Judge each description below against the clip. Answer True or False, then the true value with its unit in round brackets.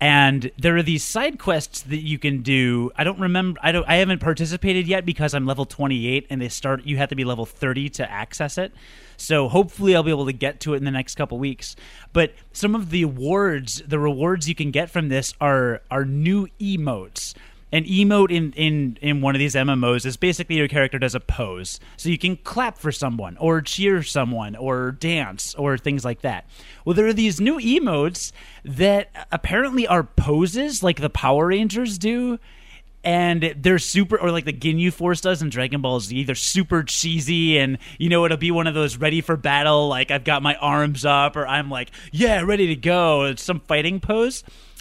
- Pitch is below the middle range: False (150 Hz)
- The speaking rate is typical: False (210 wpm)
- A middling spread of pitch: True (4.7 semitones)